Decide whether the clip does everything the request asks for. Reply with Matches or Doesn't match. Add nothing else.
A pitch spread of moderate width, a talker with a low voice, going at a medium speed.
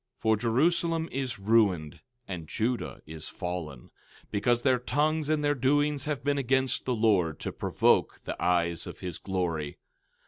Doesn't match